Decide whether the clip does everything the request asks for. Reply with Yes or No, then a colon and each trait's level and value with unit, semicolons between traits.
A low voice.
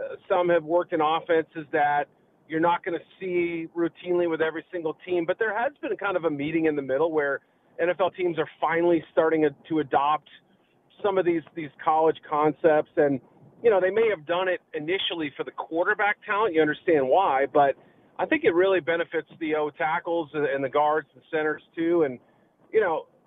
No: medium, 165 Hz